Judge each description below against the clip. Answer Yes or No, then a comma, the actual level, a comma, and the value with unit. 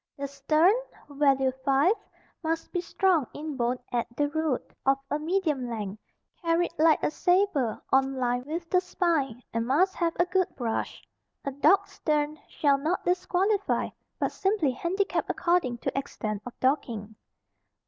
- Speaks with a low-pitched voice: No, very high, 295 Hz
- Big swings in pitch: No, average, 5.0 semitones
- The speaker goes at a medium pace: Yes, average, 150 wpm